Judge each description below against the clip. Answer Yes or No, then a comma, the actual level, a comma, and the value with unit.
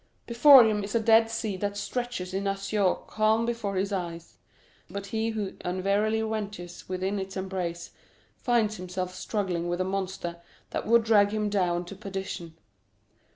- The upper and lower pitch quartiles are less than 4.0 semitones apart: Yes, average, 3.0 semitones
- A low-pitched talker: No, high, 200 Hz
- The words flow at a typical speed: Yes, average, 155 wpm